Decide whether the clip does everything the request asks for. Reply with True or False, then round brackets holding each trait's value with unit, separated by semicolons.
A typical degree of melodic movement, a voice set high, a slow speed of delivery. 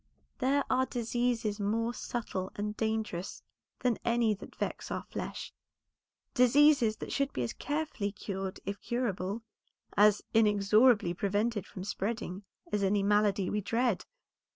True (3.1 semitones; 215 Hz; 130 wpm)